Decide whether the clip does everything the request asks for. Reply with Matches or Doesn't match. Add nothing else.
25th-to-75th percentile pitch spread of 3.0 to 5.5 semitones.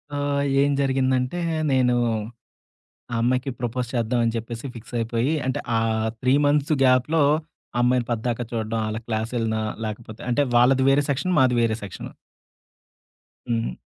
Doesn't match